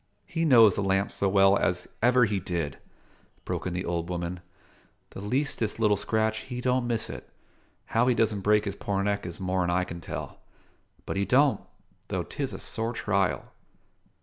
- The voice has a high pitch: No, low, 100 Hz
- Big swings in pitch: No, average, 3.8 semitones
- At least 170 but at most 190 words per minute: Yes, average, 180 wpm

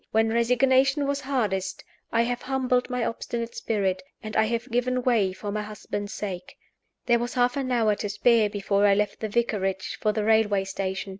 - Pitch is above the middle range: Yes, high, 225 Hz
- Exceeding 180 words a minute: Yes, average, 190 wpm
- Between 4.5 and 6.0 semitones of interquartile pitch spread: No, average, 3.3 semitones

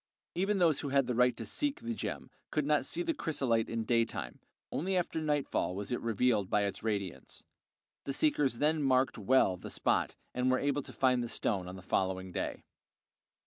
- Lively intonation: Yes, wide, 6.1 semitones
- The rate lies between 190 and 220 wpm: Yes, average, 195 wpm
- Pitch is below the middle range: Yes, low, 125 Hz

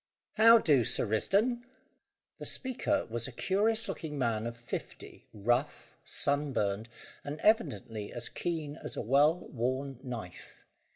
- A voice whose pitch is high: No, low, 135 Hz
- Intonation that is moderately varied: No, wide, 6.6 semitones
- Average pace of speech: No, slow, 130 wpm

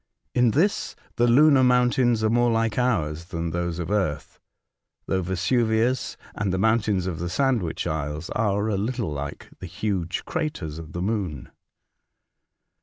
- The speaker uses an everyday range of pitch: No, wide, 6.0 semitones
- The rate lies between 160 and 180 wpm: No, average, 150 wpm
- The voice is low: Yes, low, 105 Hz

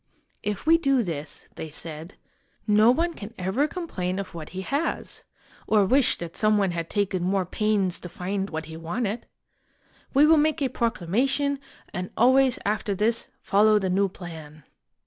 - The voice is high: Yes, high, 205 Hz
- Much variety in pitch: Yes, wide, 5.7 semitones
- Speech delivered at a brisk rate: No, average, 175 wpm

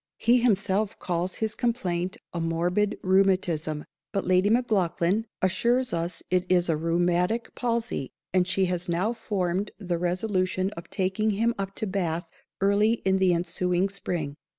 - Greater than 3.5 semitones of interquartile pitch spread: No, average, 3.0 semitones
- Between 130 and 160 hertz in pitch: No, medium, 185 Hz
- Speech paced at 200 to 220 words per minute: No, average, 150 wpm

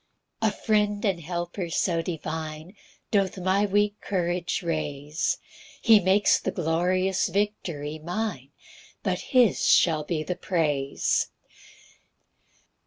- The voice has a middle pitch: Yes, medium, 175 Hz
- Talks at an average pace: No, slow, 110 wpm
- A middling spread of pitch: Yes, average, 4.0 semitones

